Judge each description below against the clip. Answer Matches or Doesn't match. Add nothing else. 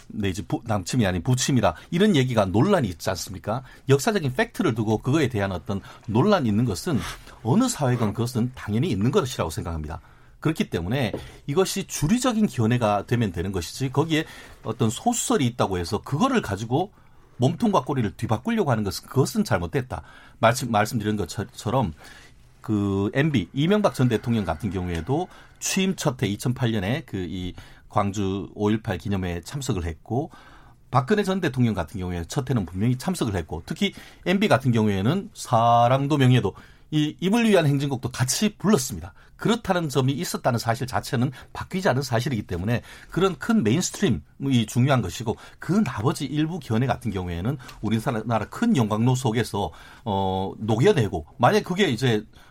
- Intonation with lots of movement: Matches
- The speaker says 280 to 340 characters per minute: Doesn't match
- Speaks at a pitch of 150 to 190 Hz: Doesn't match